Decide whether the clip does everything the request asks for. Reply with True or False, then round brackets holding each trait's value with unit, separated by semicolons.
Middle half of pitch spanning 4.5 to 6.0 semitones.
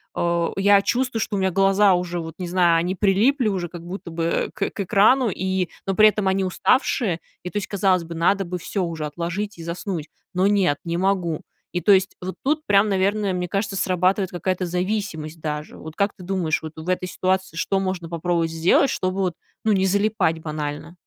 False (2.7 semitones)